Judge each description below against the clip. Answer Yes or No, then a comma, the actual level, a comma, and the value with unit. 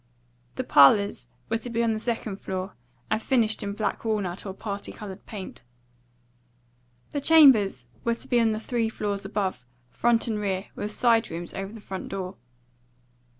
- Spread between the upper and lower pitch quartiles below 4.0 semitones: Yes, average, 2.8 semitones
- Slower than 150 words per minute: No, average, 170 wpm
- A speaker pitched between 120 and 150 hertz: No, high, 210 Hz